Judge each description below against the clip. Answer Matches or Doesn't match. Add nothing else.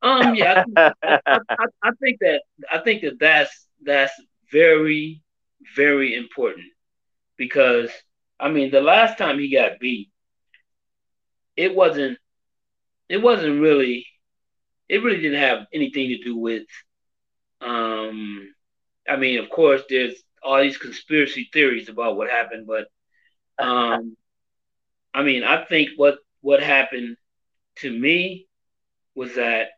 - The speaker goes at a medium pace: Matches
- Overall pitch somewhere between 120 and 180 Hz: Matches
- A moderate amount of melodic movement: Matches